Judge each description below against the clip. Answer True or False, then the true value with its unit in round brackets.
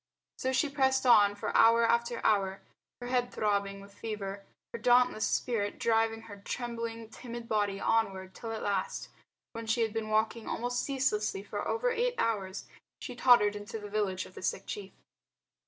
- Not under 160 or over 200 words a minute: True (170 wpm)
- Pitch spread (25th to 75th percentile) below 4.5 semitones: True (2.9 semitones)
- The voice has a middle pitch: False (225 Hz)